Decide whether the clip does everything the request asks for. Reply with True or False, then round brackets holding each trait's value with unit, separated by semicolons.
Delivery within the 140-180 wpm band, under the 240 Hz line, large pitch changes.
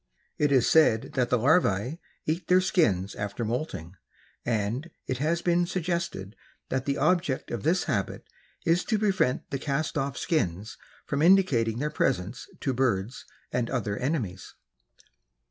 True (145 wpm; 135 Hz; 6.7 semitones)